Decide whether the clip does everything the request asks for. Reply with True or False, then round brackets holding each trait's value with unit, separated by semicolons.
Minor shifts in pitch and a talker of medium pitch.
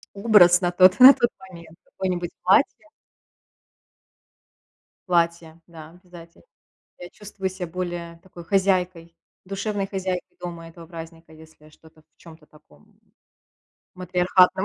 True (2.1 semitones; 175 Hz)